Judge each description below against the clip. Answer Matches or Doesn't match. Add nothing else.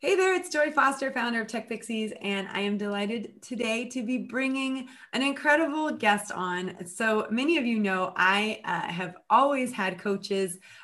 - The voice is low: Doesn't match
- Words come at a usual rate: Matches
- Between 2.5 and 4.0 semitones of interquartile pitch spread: Doesn't match